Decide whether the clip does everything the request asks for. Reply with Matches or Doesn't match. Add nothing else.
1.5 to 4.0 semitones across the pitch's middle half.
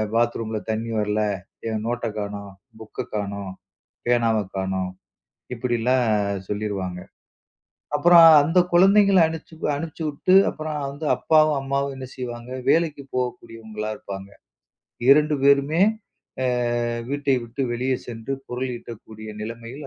Doesn't match